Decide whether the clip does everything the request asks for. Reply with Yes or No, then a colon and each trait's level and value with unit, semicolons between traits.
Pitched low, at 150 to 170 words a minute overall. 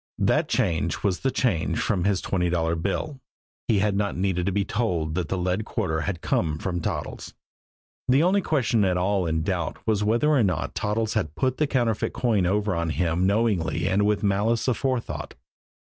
No: low, 100 Hz; average, 190 wpm